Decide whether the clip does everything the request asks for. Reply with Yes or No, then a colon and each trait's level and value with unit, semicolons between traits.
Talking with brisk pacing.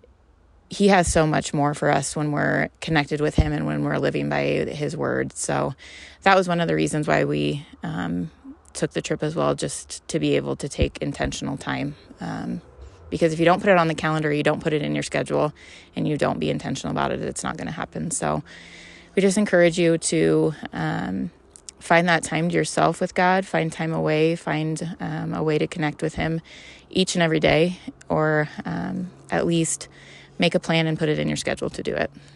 Yes: fast, 215 wpm